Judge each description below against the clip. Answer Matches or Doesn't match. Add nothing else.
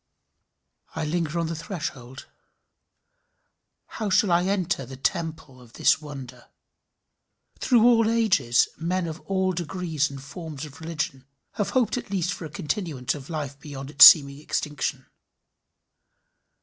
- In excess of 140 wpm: Doesn't match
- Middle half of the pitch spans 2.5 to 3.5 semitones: Doesn't match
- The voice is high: Doesn't match